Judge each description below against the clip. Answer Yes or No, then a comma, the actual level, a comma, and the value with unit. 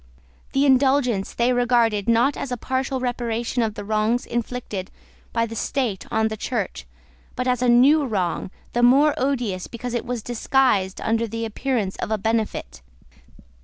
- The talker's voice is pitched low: No, high, 235 Hz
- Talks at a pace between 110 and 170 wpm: Yes, average, 165 wpm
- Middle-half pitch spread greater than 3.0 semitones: No, narrow, 2.5 semitones